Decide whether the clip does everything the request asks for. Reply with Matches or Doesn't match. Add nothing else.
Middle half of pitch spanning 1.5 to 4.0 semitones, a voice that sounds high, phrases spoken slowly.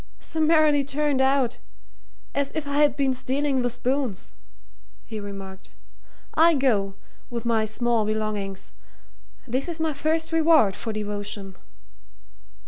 Doesn't match